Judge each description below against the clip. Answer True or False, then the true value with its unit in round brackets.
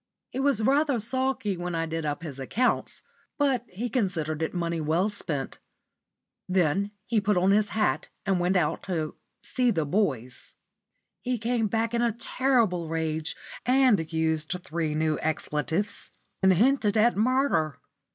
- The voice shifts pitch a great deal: True (6.6 semitones)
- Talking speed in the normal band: True (150 wpm)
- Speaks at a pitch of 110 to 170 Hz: False (190 Hz)